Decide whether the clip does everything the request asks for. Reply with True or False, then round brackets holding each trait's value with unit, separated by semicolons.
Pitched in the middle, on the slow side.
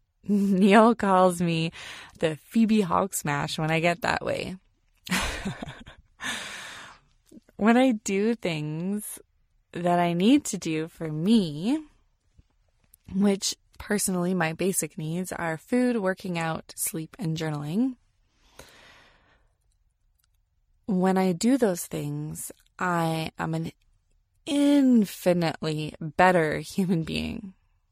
True (175 Hz; 100 wpm)